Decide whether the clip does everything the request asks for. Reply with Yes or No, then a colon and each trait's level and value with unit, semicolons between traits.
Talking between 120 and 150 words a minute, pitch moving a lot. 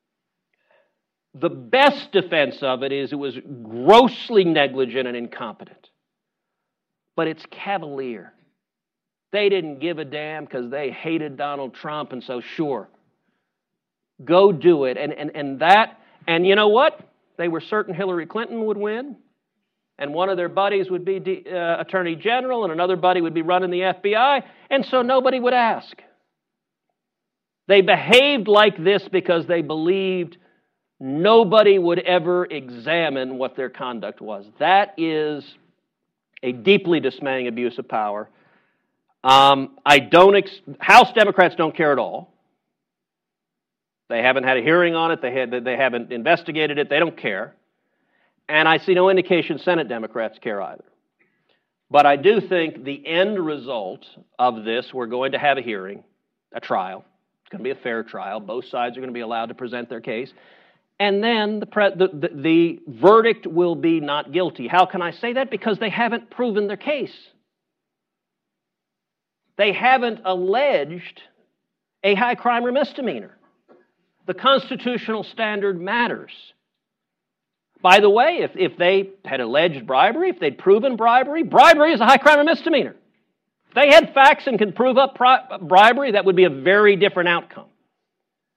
No: average, 160 wpm; wide, 5.7 semitones